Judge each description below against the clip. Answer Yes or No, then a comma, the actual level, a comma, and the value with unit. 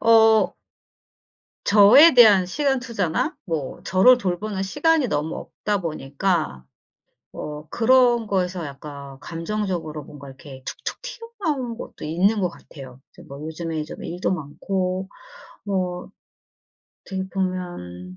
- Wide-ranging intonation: Yes, wide, 6.0 semitones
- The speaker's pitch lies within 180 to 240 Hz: Yes, medium, 185 Hz